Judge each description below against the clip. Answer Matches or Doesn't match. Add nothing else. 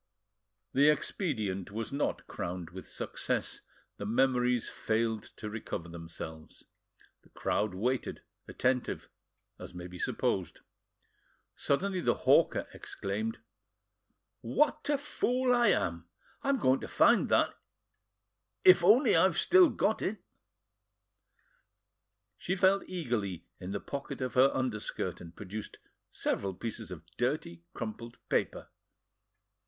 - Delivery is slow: Matches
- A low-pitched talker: Matches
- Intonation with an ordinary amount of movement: Doesn't match